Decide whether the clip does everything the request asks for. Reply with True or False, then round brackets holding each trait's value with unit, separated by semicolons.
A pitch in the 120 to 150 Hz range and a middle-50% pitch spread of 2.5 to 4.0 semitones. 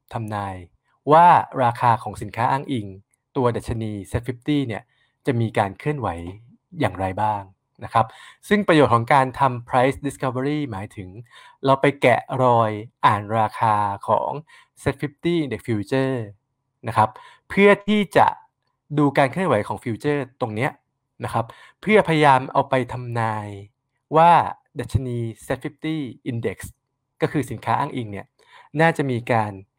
False (125 Hz; 4.5 semitones)